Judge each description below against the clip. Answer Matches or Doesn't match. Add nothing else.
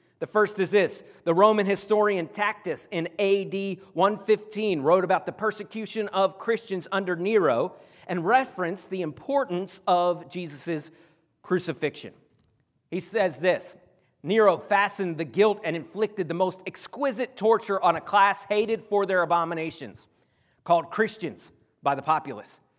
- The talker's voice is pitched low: Doesn't match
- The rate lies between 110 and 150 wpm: Matches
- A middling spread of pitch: Matches